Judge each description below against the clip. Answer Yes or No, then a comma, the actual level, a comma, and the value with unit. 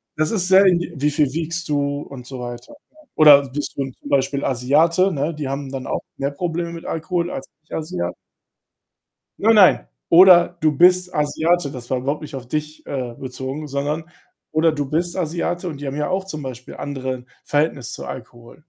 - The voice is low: No, medium, 150 Hz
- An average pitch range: Yes, average, 3.9 semitones